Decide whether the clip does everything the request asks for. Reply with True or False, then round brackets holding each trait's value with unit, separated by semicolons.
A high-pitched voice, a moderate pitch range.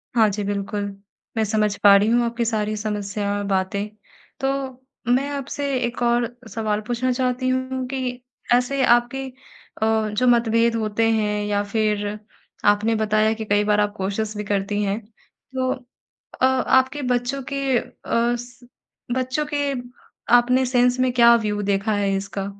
True (230 Hz; 3.3 semitones)